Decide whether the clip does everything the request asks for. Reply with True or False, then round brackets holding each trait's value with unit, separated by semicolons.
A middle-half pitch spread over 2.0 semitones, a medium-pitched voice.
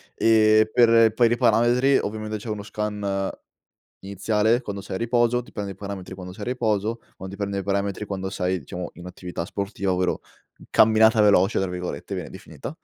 False (2.7 semitones; 105 Hz)